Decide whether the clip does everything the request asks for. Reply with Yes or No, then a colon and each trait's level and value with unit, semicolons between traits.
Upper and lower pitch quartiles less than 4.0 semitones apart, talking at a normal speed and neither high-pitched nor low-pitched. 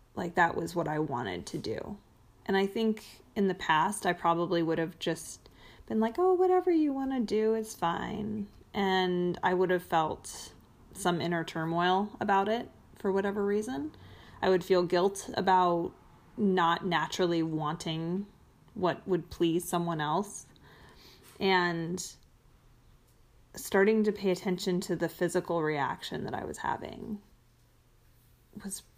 Yes: average, 3.5 semitones; average, 145 wpm; medium, 180 Hz